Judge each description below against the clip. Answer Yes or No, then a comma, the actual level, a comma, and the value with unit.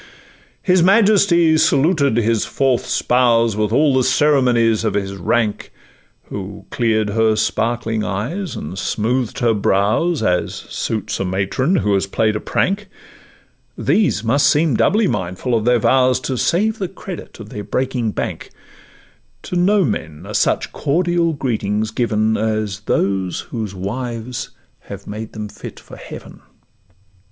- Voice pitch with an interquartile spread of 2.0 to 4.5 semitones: No, wide, 5.4 semitones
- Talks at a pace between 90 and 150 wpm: Yes, average, 145 wpm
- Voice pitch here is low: Yes, low, 115 Hz